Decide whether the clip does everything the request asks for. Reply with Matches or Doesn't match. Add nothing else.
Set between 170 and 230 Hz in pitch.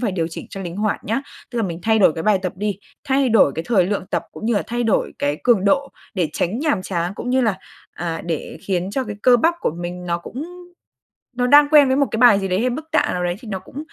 Matches